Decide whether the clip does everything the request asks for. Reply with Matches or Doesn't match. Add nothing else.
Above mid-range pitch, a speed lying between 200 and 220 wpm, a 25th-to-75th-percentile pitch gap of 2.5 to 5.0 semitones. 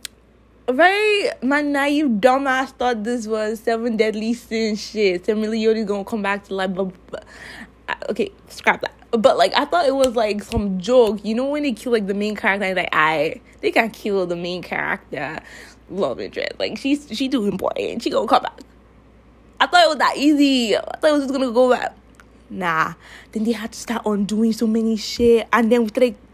Matches